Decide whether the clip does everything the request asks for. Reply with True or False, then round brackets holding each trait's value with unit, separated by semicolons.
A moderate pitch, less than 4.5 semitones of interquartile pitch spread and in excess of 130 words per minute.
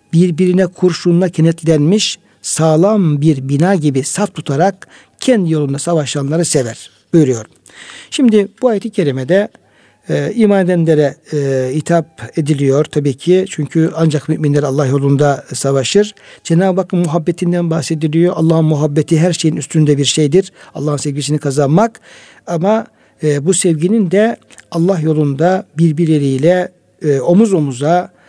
False (165 Hz; 3.7 semitones; 120 wpm)